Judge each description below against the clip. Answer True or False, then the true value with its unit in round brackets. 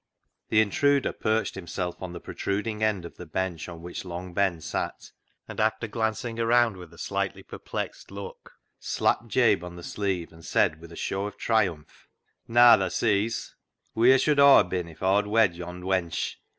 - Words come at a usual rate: True (195 wpm)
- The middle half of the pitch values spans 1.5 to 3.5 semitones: False (4.0 semitones)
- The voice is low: True (95 Hz)